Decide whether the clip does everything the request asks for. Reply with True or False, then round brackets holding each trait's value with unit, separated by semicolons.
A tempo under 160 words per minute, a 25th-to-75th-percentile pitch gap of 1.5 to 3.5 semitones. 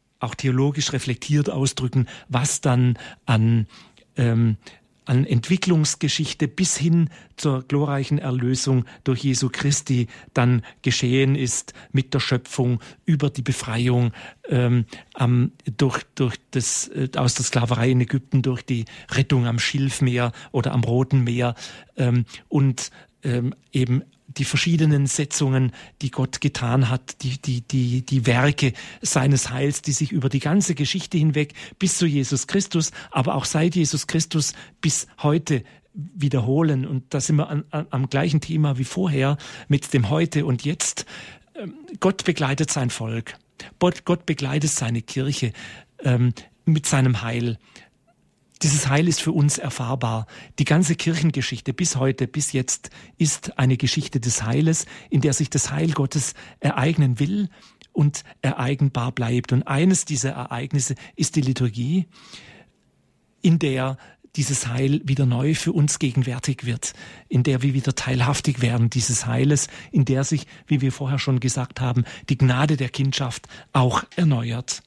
True (145 wpm; 3.0 semitones)